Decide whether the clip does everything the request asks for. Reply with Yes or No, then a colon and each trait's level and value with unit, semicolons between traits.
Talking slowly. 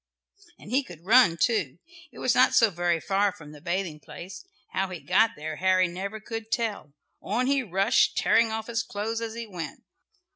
No: average, 190 wpm